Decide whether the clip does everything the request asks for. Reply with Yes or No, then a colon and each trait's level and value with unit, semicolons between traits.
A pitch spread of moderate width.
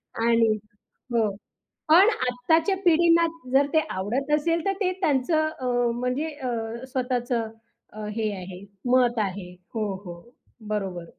No: wide, 6.2 semitones